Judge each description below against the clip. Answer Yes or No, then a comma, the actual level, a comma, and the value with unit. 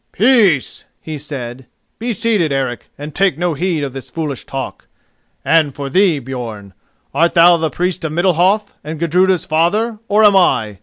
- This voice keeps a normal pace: Yes, average, 165 wpm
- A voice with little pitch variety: No, wide, 5.4 semitones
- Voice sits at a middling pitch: Yes, medium, 165 Hz